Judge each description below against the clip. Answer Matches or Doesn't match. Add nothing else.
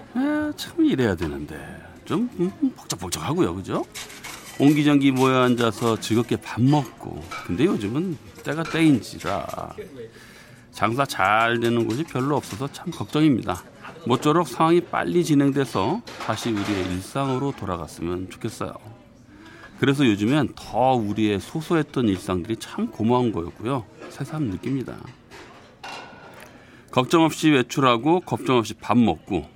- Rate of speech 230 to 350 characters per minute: Matches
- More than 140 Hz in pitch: Doesn't match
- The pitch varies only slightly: Doesn't match